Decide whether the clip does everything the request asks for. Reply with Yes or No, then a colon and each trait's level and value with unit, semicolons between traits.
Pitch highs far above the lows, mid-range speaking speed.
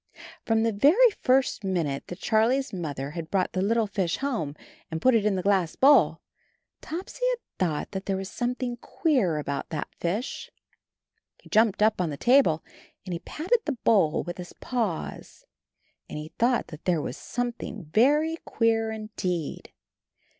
Yes: wide, 6.3 semitones; average, 165 wpm